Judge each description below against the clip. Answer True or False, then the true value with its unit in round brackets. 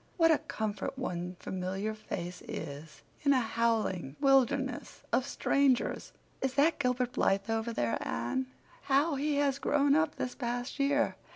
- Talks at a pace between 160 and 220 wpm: False (150 wpm)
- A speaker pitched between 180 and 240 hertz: False (250 Hz)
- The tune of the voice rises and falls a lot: True (5.9 semitones)